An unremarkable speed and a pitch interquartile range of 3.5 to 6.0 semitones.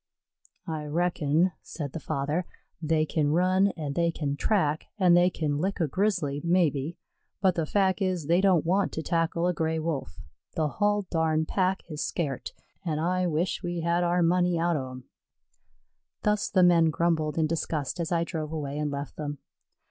No: average, 180 wpm; average, 2.8 semitones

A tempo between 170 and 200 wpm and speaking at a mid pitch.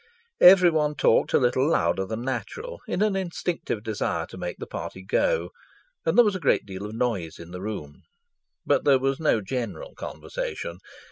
No: average, 180 wpm; low, 130 Hz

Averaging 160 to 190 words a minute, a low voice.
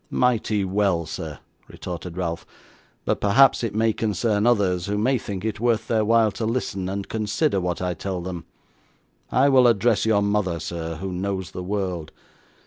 Yes: average, 170 wpm; low, 100 Hz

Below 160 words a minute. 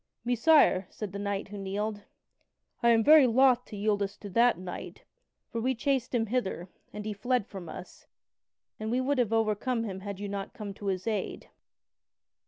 No: average, 190 wpm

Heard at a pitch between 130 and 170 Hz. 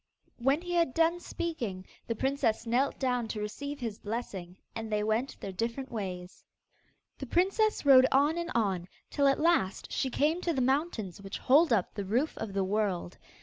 No: high, 245 Hz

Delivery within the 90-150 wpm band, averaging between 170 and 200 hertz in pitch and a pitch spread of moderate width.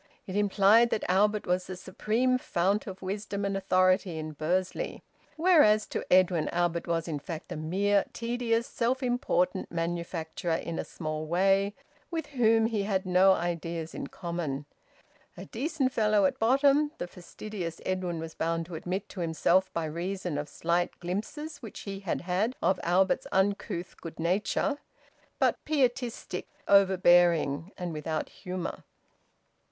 Yes: average, 145 wpm; medium, 185 Hz; average, 3.8 semitones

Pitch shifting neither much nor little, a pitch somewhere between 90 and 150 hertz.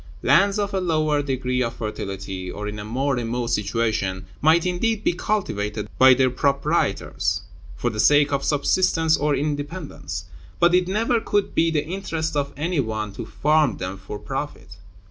No: wide, 7.2 semitones; medium, 140 Hz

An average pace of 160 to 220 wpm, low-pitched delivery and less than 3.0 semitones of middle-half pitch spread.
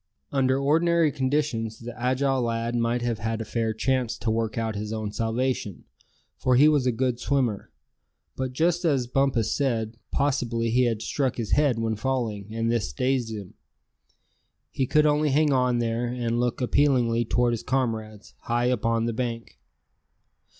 Yes: average, 170 wpm; low, 120 Hz; narrow, 2.6 semitones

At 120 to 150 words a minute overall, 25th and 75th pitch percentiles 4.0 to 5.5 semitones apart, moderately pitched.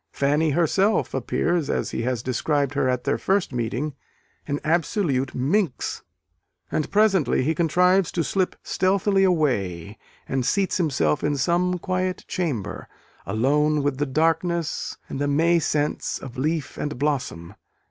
Yes: average, 140 wpm; average, 5.1 semitones; medium, 150 Hz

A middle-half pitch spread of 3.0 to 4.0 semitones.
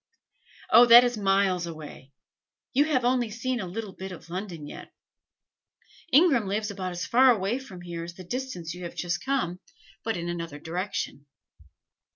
No: wide, 5.6 semitones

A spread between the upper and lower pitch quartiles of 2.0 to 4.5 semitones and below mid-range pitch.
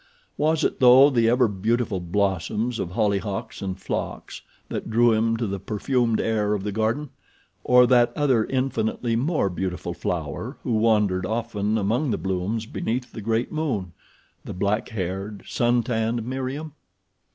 Yes: average, 3.4 semitones; low, 110 Hz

